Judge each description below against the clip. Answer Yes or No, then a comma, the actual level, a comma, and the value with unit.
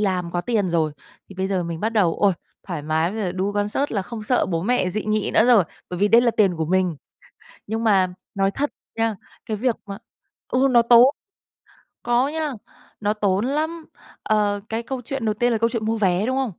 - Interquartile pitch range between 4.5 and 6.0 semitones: No, average, 4.1 semitones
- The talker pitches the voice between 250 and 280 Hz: No, high, 210 Hz